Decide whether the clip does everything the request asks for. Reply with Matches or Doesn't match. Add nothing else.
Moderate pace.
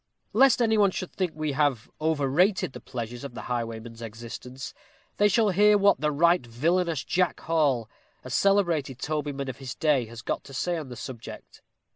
Matches